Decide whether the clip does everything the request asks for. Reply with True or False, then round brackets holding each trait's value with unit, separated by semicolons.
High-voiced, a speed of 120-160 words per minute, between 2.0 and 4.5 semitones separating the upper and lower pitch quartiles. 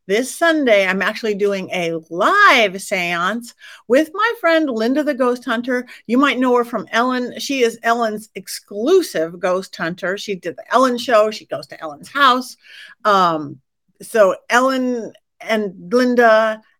True (225 Hz; 150 wpm; 4.2 semitones)